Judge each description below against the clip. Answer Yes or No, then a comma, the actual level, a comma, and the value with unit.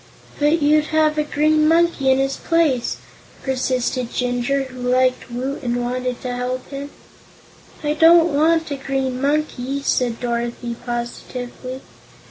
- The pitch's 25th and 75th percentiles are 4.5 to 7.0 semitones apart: No, average, 3.3 semitones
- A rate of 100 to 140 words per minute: Yes, slow, 135 wpm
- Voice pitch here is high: Yes, very high, 265 Hz